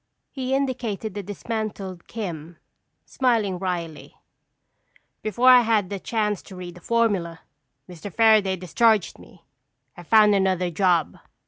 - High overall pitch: Yes, high, 200 Hz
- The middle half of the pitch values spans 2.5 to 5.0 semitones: Yes, average, 3.9 semitones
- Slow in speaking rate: Yes, slow, 125 wpm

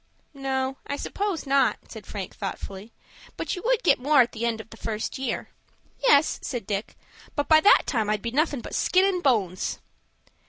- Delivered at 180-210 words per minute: Yes, average, 190 wpm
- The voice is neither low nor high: No, very high, 265 Hz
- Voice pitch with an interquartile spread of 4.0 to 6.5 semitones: Yes, wide, 5.5 semitones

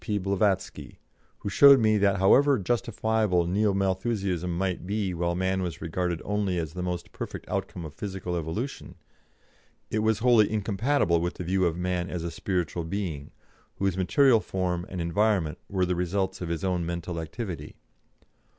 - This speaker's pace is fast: No, average, 165 wpm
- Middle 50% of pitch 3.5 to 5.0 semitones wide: No, average, 3.1 semitones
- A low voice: Yes, very low, 95 Hz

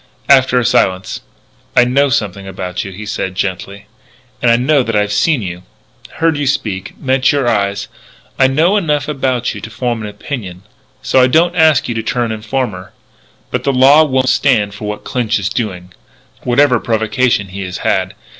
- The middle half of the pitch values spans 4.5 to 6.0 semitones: Yes, average, 4.8 semitones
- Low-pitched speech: Yes, low, 120 Hz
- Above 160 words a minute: Yes, average, 180 wpm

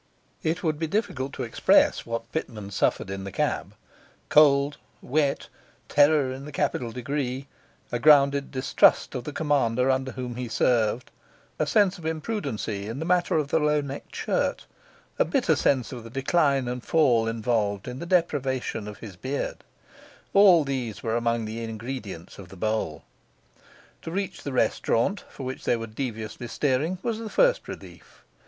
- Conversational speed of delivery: Yes, average, 165 wpm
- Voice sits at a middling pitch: No, low, 130 Hz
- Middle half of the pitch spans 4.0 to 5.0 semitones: Yes, average, 4.6 semitones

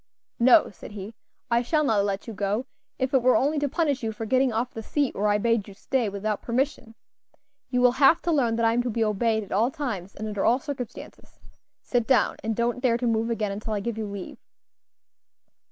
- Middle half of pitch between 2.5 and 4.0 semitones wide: Yes, average, 3.3 semitones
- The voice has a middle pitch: No, high, 230 Hz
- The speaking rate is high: Yes, fast, 225 wpm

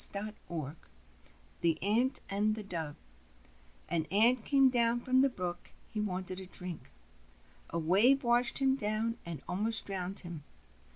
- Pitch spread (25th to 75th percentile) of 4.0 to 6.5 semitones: Yes, average, 5.0 semitones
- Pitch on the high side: Yes, high, 205 Hz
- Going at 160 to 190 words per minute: No, average, 150 wpm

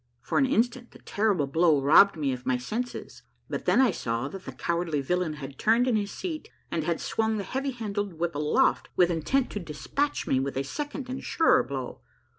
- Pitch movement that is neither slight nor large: No, wide, 8.5 semitones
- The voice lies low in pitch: No, medium, 180 Hz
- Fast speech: Yes, fast, 220 wpm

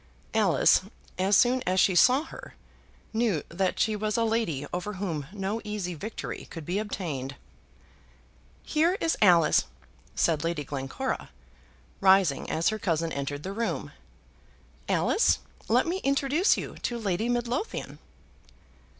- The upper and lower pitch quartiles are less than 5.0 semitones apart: No, wide, 5.6 semitones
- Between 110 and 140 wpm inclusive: Yes, slow, 135 wpm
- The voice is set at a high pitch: Yes, high, 195 Hz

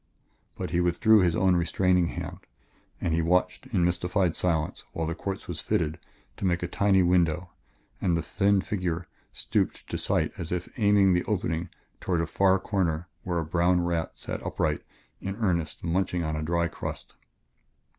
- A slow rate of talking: No, average, 175 wpm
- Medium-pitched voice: No, very low, 90 Hz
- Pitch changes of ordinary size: No, narrow, 1.9 semitones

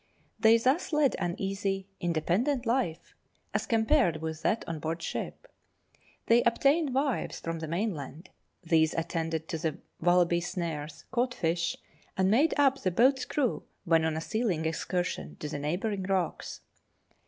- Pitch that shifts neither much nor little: No, wide, 6.4 semitones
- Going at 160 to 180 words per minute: No, average, 150 wpm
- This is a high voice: No, medium, 180 Hz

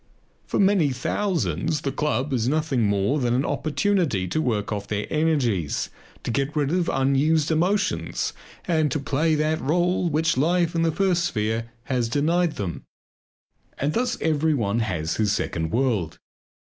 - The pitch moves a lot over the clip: Yes, wide, 6.4 semitones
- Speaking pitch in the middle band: Yes, medium, 145 Hz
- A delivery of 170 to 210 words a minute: No, average, 155 wpm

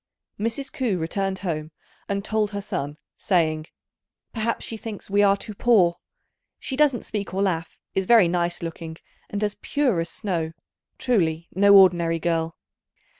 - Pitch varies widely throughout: No, average, 4.2 semitones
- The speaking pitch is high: Yes, high, 195 Hz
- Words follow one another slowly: No, average, 155 wpm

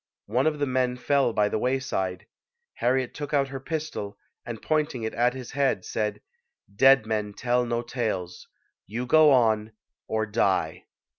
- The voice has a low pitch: Yes, low, 125 Hz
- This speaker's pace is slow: No, average, 160 wpm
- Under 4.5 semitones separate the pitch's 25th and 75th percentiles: Yes, average, 3.8 semitones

